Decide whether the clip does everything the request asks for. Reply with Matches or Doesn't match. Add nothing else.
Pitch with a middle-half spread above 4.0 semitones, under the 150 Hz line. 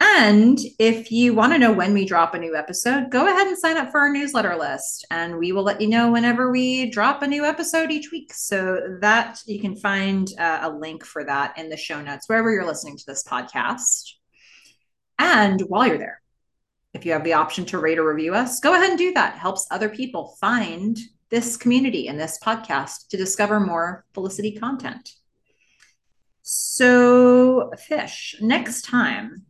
Doesn't match